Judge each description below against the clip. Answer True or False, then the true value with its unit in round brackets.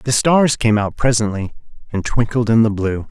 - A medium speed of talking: True (195 wpm)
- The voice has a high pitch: False (115 Hz)